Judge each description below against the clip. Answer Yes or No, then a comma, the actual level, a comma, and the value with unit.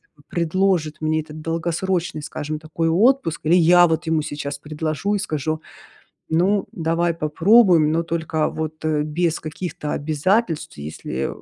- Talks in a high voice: No, medium, 160 Hz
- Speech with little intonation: Yes, narrow, 2.2 semitones